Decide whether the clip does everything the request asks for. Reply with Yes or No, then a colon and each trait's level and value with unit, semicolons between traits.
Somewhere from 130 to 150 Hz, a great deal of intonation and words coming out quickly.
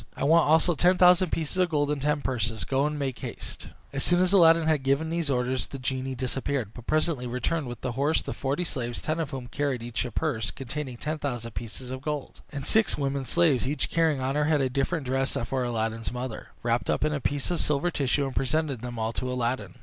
No: low, 135 Hz; average, 3.8 semitones; fast, 235 wpm